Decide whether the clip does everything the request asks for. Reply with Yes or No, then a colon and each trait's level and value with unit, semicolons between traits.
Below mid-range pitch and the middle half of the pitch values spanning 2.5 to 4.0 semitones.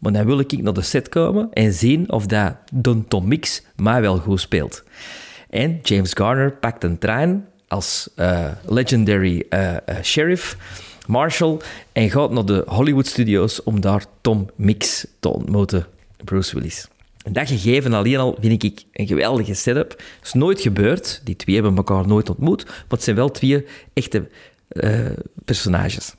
No: low, 110 Hz; average, 4.9 semitones